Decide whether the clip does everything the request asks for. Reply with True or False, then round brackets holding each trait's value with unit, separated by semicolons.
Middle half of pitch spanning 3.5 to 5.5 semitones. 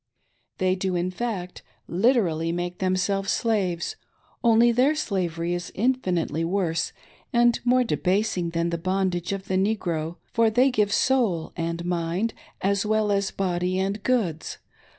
True (4.0 semitones)